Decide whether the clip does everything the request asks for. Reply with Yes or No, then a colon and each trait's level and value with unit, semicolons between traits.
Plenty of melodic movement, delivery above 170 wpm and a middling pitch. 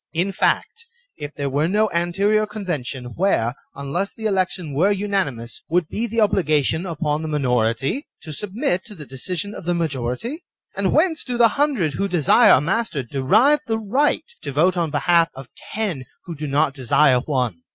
Yes: wide, 6.7 semitones; average, 180 wpm; medium, 170 Hz